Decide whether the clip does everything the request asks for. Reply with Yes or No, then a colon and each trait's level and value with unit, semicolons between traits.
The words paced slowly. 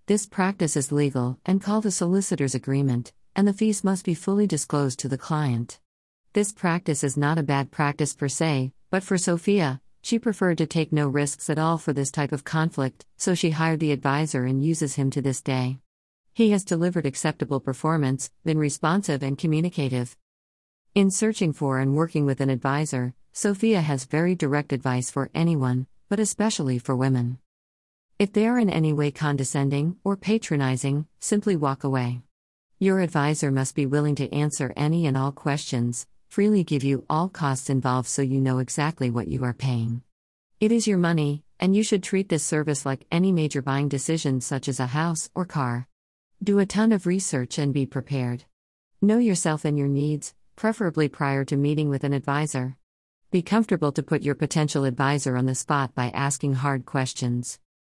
No: average, 180 wpm